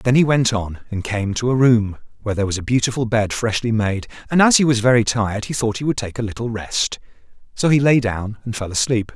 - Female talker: No, male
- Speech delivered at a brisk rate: Yes, fast, 250 wpm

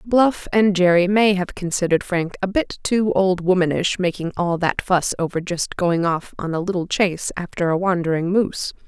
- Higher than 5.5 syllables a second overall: No, 5.0 syllables/s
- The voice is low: No, medium, 180 Hz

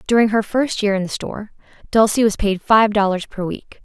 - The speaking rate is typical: No, fast, 220 wpm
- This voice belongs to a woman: Yes, female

